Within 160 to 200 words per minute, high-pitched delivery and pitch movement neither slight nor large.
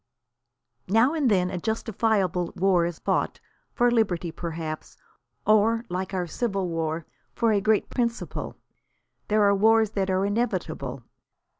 No: slow, 135 wpm; high, 195 Hz; average, 4.0 semitones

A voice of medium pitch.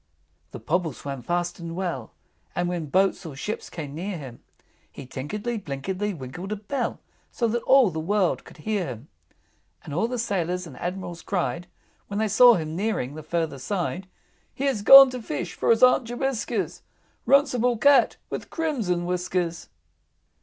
Yes: medium, 180 Hz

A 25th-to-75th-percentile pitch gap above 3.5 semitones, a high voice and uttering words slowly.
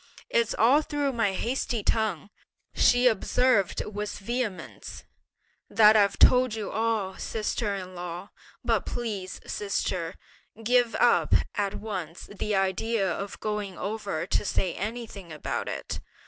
No: average, 3.2 semitones; high, 210 Hz; slow, 130 wpm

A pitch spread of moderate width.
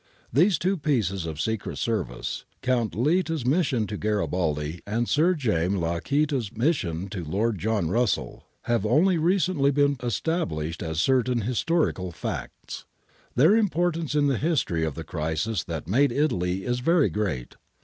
No: wide, 8.9 semitones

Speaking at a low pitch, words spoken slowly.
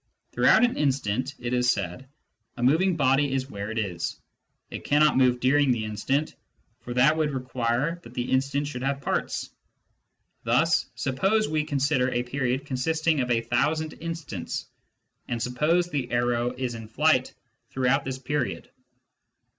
No: low, 130 Hz; average, 155 wpm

